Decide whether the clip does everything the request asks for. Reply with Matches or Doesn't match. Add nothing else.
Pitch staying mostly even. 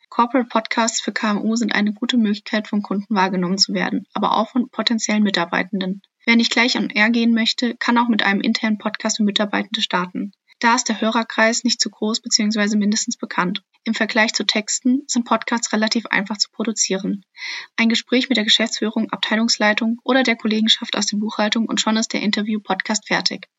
Matches